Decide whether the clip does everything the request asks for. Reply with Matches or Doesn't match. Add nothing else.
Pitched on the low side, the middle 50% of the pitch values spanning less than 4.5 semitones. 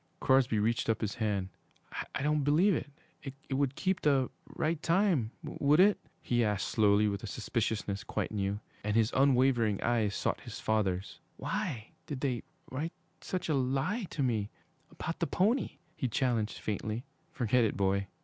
Doesn't match